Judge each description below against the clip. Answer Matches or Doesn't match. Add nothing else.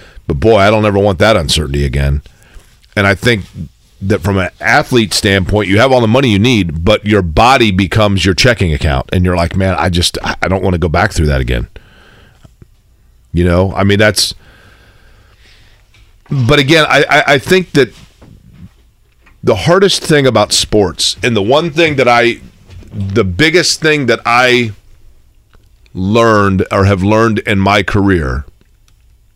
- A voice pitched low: Matches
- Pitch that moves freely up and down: Doesn't match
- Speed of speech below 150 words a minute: Doesn't match